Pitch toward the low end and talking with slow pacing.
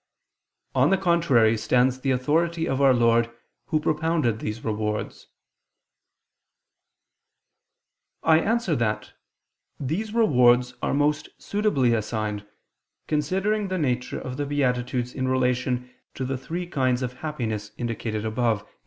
Yes: low, 130 Hz; slow, 125 wpm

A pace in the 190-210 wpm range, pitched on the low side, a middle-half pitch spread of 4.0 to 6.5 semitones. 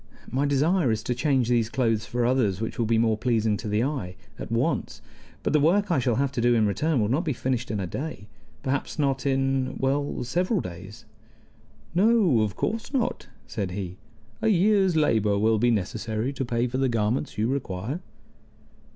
Yes: average, 195 wpm; low, 125 Hz; average, 4.7 semitones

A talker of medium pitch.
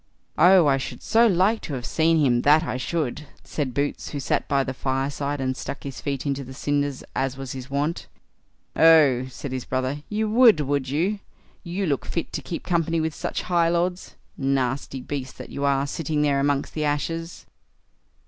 Yes: medium, 145 Hz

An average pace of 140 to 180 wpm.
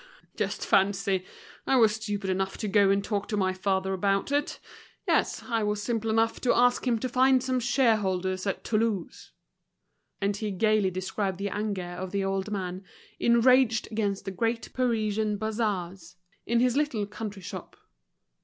Yes: average, 165 wpm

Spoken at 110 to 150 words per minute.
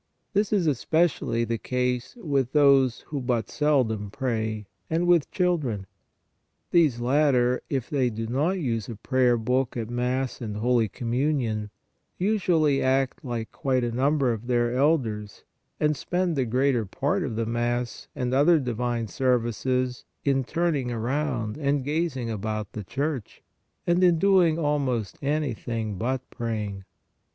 Yes: average, 145 wpm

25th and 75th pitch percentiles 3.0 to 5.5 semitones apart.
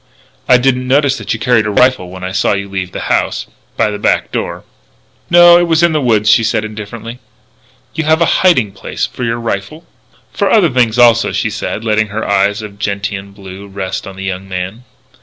Yes: average, 4.4 semitones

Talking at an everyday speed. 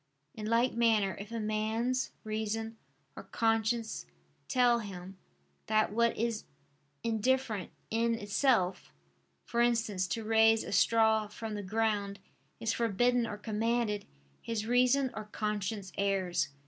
No: slow, 125 wpm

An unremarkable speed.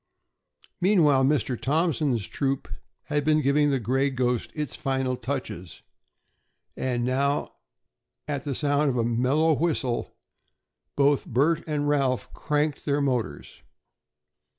No: slow, 120 wpm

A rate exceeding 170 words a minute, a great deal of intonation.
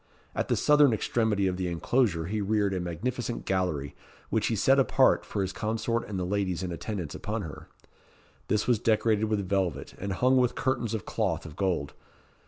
No: average, 190 wpm; average, 3.7 semitones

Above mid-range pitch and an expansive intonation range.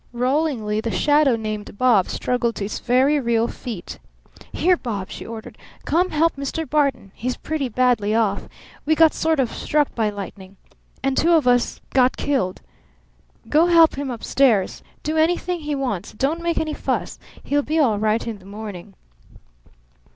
Yes: very high, 255 Hz; wide, 5.9 semitones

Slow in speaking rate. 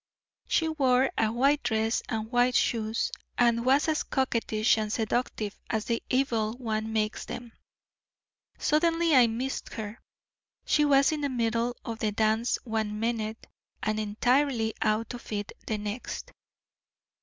No: average, 145 wpm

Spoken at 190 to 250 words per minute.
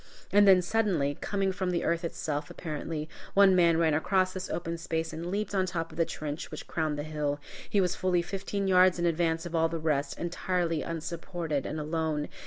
Yes: average, 200 wpm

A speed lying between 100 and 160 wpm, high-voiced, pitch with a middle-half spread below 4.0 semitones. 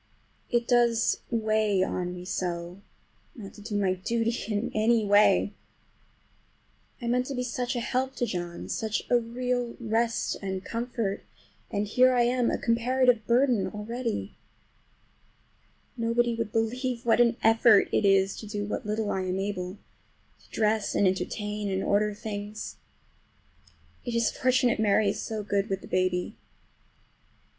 Yes: average, 150 wpm; high, 220 Hz; average, 2.8 semitones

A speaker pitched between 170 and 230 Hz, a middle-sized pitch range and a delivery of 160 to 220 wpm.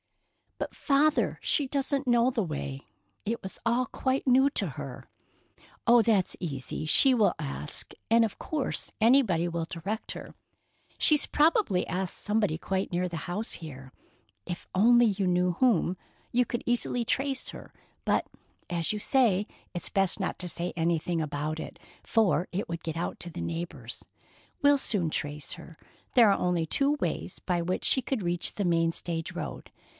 No: high, 190 Hz; wide, 6.2 semitones; average, 170 wpm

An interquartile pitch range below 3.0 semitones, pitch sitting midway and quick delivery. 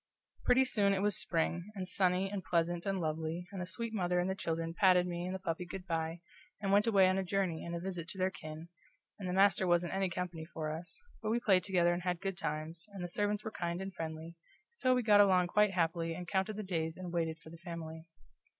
Yes: narrow, 2.5 semitones; medium, 180 Hz; fast, 240 wpm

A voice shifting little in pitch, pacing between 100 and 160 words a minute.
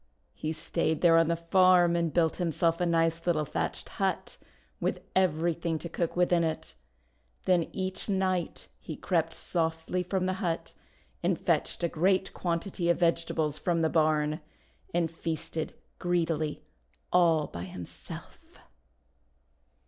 Yes: narrow, 1.7 semitones; average, 140 wpm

